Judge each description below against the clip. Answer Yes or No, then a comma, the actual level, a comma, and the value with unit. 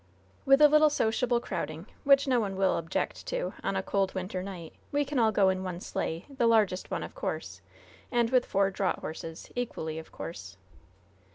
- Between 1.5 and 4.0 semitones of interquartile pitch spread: No, wide, 5.5 semitones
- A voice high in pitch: Yes, high, 200 Hz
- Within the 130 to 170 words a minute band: No, average, 190 wpm